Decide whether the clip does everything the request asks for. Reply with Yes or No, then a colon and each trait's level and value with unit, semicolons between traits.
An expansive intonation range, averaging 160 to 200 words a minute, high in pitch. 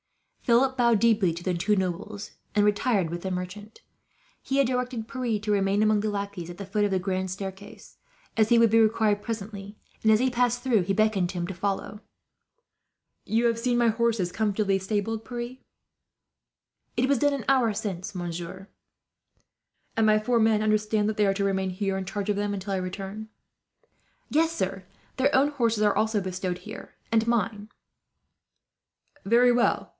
No: average, 3.1 semitones; average, 180 wpm; high, 210 Hz